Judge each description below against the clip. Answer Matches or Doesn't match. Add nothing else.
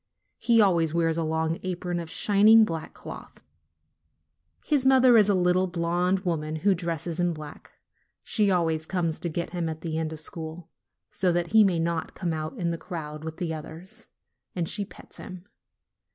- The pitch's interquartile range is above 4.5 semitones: Doesn't match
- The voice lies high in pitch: Doesn't match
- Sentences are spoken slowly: Doesn't match